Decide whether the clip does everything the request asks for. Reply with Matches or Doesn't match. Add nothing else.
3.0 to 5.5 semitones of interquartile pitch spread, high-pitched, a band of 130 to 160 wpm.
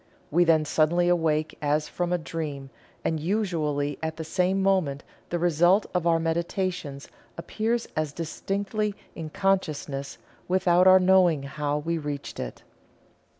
Doesn't match